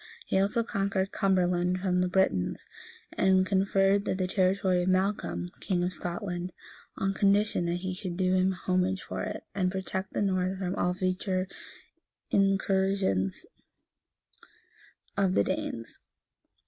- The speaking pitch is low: No, medium, 185 Hz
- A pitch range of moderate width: No, narrow, 1.2 semitones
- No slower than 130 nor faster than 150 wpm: Yes, slow, 135 wpm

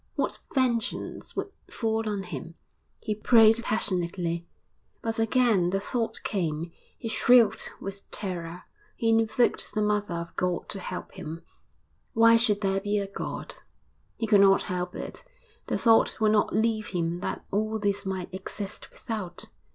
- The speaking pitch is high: Yes, high, 205 Hz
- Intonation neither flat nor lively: Yes, average, 3.6 semitones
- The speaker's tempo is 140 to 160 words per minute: Yes, average, 150 wpm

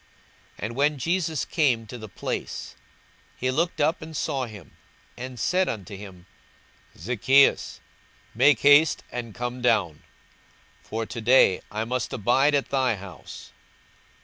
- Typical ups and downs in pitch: Yes, average, 4.7 semitones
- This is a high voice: No, low, 125 Hz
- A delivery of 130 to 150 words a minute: Yes, average, 140 wpm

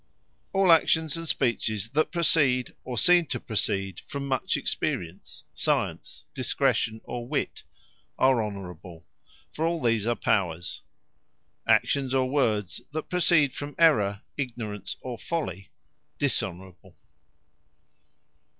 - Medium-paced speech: No, slow, 115 wpm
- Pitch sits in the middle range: No, low, 125 Hz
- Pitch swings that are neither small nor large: No, wide, 6.7 semitones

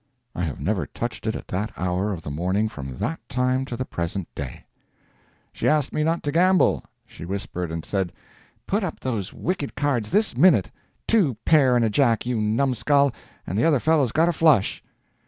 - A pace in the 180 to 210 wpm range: Yes, average, 190 wpm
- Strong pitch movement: Yes, wide, 7.5 semitones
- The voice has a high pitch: No, low, 120 Hz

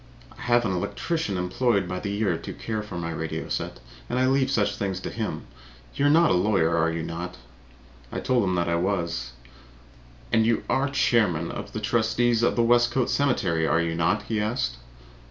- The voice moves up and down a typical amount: No, wide, 6.0 semitones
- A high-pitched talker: No, low, 100 Hz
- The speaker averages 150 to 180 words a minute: No, average, 195 wpm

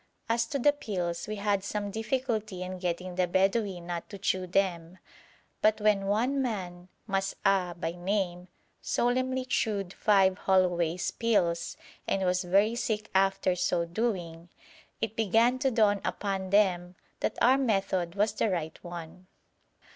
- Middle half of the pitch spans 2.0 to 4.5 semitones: Yes, average, 3.4 semitones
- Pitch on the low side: No, high, 195 Hz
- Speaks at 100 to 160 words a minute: Yes, average, 145 wpm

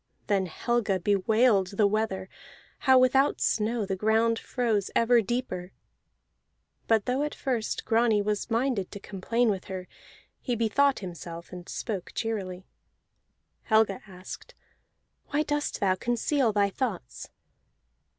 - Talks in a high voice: Yes, high, 215 Hz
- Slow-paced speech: Yes, slow, 125 wpm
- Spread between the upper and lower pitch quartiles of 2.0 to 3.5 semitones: No, average, 4.0 semitones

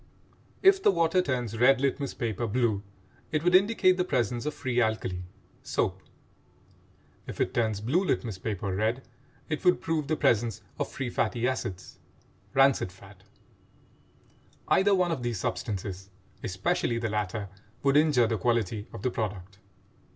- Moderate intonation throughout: No, wide, 6.2 semitones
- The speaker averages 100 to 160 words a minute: Yes, average, 150 wpm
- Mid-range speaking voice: No, low, 120 Hz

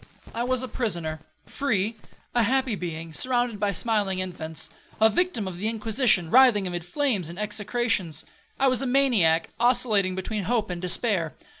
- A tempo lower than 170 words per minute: Yes, average, 145 wpm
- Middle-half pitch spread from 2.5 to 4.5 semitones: No, average, 5.3 semitones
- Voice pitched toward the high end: Yes, high, 210 Hz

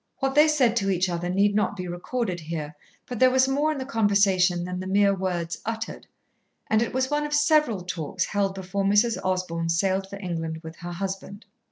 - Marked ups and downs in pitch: No, average, 4.6 semitones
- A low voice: No, high, 195 Hz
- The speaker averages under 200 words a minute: No, fast, 205 wpm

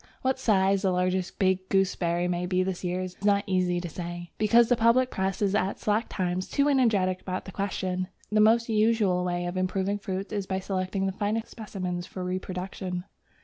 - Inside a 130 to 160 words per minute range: No, average, 195 wpm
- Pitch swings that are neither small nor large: No, narrow, 2.2 semitones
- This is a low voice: No, high, 190 Hz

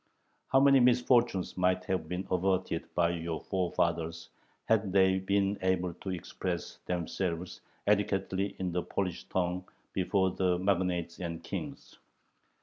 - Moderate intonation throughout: No, narrow, 2.0 semitones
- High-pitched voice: No, very low, 90 Hz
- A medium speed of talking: No, slow, 130 wpm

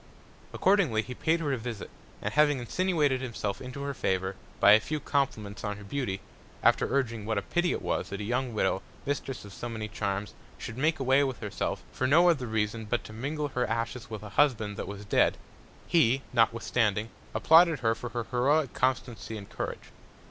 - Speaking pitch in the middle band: No, low, 120 Hz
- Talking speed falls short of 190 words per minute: No, average, 195 wpm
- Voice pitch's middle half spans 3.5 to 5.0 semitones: Yes, average, 4.7 semitones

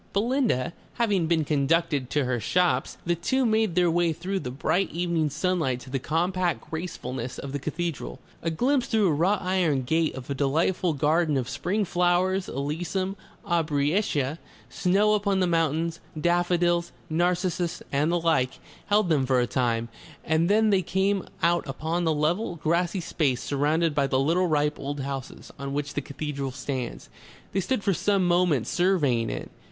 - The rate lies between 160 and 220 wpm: Yes, average, 165 wpm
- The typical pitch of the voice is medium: Yes, medium, 165 Hz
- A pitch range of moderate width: Yes, average, 4.3 semitones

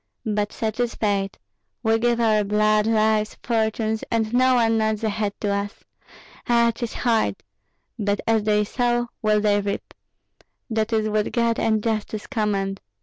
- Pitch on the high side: Yes, high, 220 Hz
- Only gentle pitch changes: Yes, narrow, 1.5 semitones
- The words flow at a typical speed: Yes, average, 160 wpm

